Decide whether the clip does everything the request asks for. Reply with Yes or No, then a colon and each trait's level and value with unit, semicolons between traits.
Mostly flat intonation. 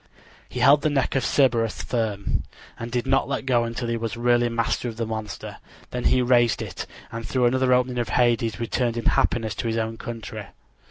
Yes: narrow, 1.6 semitones